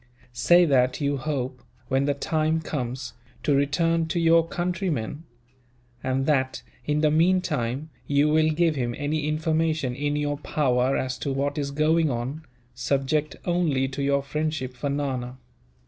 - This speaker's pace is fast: No, average, 150 wpm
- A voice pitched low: No, medium, 145 Hz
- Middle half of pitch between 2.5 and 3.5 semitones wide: Yes, average, 2.9 semitones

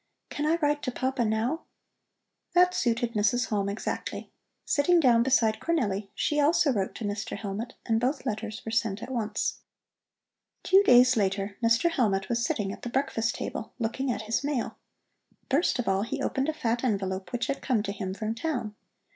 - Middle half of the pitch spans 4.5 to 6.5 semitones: No, average, 4.1 semitones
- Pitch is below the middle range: No, high, 235 Hz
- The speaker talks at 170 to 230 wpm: Yes, average, 180 wpm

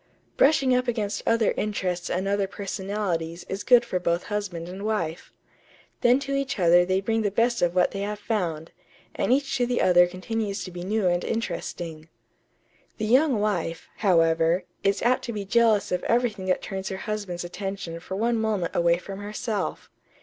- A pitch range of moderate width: Yes, average, 4.1 semitones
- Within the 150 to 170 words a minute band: No, average, 180 wpm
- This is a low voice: No, high, 200 Hz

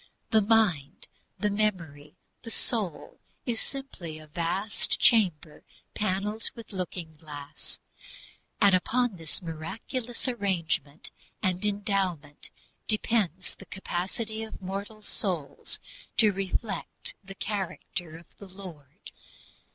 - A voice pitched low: No, high, 190 Hz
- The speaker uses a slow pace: Yes, slow, 105 wpm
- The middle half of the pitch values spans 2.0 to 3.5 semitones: No, average, 4.6 semitones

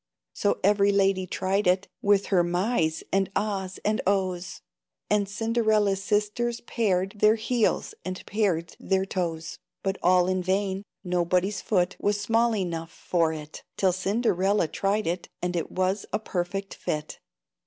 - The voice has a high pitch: Yes, high, 195 Hz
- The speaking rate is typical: Yes, average, 145 wpm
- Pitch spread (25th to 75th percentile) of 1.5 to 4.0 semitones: Yes, narrow, 2.4 semitones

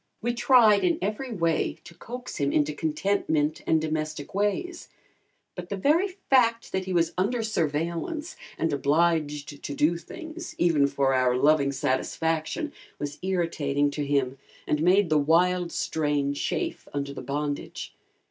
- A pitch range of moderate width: No, wide, 5.9 semitones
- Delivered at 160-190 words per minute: No, average, 150 wpm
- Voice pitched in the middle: Yes, medium, 165 Hz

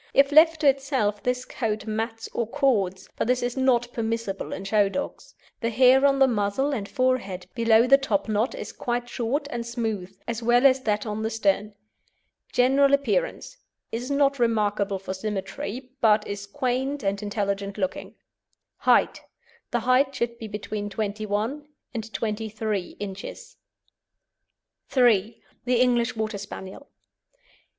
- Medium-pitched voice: No, high, 230 Hz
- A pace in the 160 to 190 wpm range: No, average, 145 wpm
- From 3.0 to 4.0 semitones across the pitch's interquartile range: Yes, average, 3.7 semitones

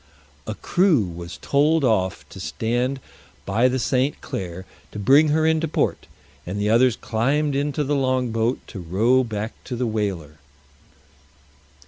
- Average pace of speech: Yes, average, 150 wpm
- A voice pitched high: No, low, 120 Hz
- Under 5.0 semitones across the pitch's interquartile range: No, average, 5.3 semitones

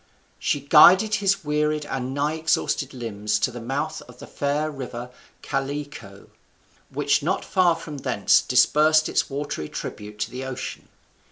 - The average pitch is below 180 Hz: Yes, medium, 140 Hz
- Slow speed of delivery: No, average, 150 wpm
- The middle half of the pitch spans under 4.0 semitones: Yes, average, 3.5 semitones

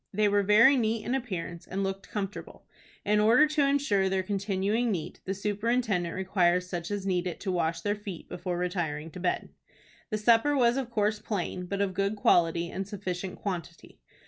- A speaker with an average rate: Yes, average, 185 wpm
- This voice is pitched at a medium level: No, high, 195 Hz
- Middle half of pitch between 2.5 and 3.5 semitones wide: Yes, average, 3.0 semitones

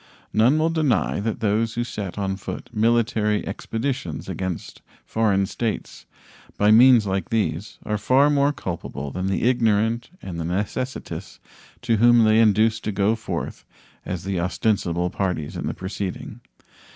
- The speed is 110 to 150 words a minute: Yes, average, 145 wpm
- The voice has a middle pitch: No, low, 110 Hz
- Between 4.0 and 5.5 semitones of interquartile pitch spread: No, average, 3.3 semitones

